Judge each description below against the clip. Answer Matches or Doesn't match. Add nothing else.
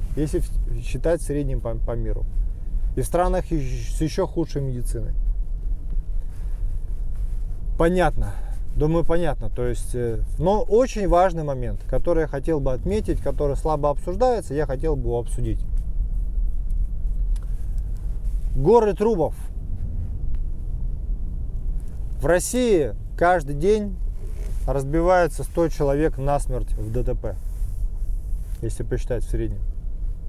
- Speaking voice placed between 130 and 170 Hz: Doesn't match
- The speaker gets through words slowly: Matches